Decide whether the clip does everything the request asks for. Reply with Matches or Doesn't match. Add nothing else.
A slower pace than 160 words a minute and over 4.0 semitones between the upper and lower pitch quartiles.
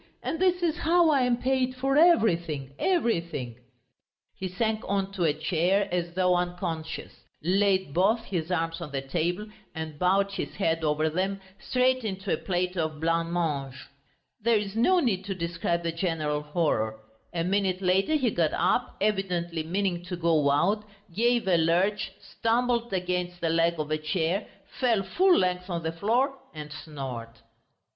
Doesn't match